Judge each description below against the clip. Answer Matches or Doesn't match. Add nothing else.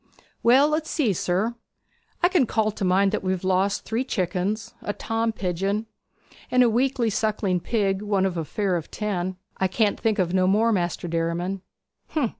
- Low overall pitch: Doesn't match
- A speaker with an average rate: Matches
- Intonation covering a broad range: Doesn't match